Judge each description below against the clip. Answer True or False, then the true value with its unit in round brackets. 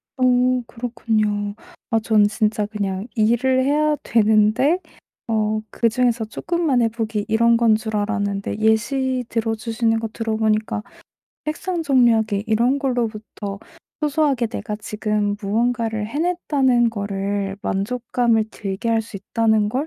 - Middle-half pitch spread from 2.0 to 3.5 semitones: True (2.7 semitones)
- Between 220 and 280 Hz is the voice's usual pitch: True (225 Hz)